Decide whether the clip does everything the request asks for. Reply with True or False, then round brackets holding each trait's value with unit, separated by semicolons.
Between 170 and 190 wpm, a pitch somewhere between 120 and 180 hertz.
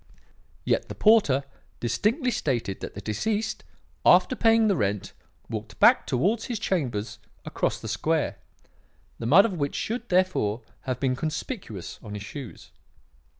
False (145 wpm; 140 Hz)